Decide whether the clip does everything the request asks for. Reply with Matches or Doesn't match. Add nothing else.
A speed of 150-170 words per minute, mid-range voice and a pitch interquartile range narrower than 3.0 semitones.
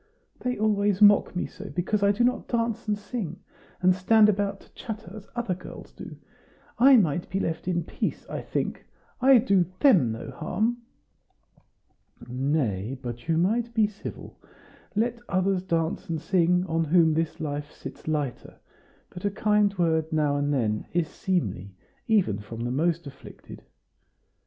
Doesn't match